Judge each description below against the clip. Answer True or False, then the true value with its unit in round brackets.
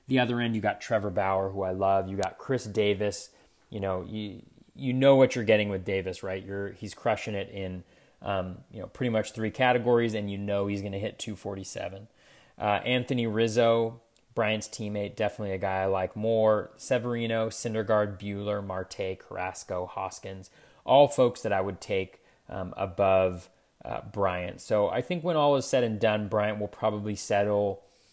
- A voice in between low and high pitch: False (105 Hz)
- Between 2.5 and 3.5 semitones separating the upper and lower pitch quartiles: True (2.9 semitones)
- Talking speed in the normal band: True (180 wpm)